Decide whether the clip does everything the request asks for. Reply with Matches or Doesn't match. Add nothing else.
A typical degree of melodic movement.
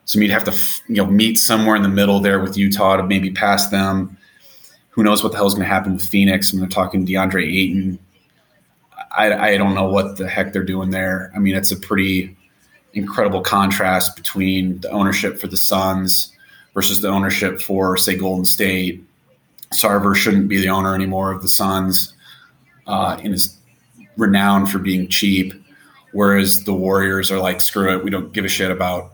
Doesn't match